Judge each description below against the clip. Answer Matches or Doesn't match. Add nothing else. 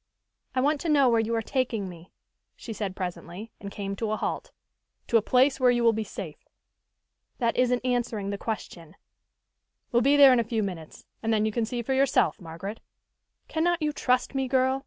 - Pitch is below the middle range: Doesn't match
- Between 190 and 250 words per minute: Matches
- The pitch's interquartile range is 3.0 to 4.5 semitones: Matches